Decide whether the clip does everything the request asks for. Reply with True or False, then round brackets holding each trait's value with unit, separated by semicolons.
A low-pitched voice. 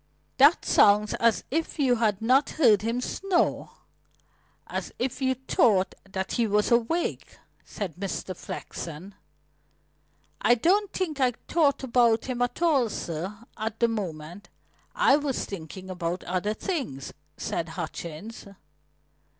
False (225 Hz)